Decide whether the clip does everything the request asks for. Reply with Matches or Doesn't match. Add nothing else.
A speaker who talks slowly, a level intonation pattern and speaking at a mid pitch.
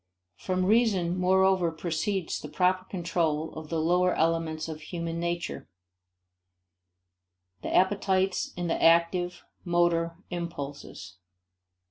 Matches